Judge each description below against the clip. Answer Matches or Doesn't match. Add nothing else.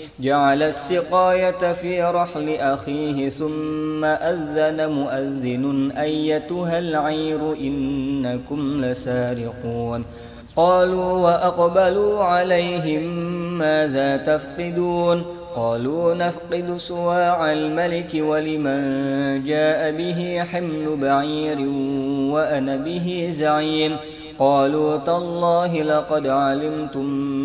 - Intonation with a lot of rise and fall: Doesn't match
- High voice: Doesn't match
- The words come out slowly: Matches